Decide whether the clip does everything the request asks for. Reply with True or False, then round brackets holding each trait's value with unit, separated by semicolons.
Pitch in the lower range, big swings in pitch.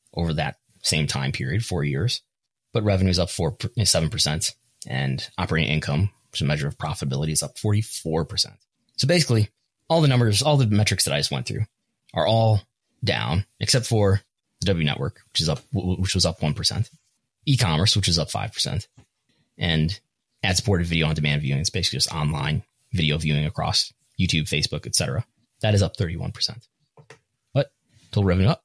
True (100 Hz; 6.5 semitones)